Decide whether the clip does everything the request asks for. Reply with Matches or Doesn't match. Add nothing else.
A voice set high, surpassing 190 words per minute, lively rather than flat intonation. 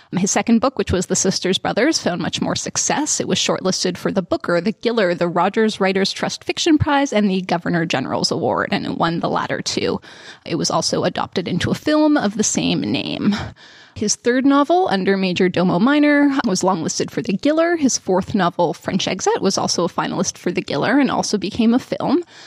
Matches